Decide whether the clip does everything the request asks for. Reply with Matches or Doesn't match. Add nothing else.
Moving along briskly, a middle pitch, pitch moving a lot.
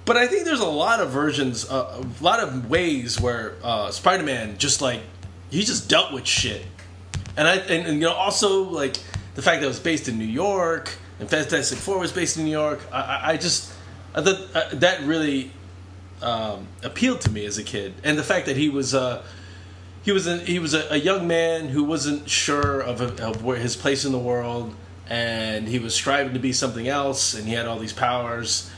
Doesn't match